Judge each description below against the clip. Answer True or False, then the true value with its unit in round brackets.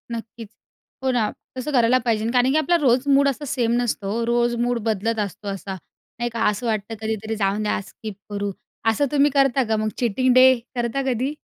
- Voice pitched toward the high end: True (235 Hz)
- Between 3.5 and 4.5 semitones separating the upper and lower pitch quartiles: False (2.9 semitones)